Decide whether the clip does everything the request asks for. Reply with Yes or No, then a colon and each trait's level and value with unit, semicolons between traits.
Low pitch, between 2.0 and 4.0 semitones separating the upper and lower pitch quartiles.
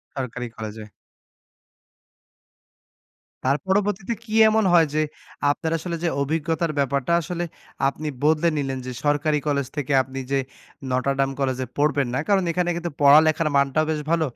No: medium, 150 Hz; average, 3.5 semitones